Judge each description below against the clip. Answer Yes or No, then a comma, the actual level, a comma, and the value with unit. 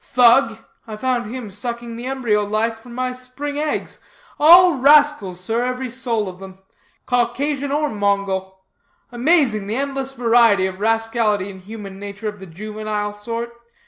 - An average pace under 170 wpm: Yes, average, 150 wpm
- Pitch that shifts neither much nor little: Yes, average, 3.7 semitones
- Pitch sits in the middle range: No, high, 230 Hz